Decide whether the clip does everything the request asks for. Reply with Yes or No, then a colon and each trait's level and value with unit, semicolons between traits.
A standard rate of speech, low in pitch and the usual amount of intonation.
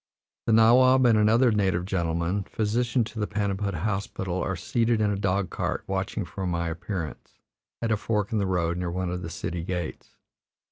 Yes: average, 185 wpm; low, 100 Hz; average, 3.7 semitones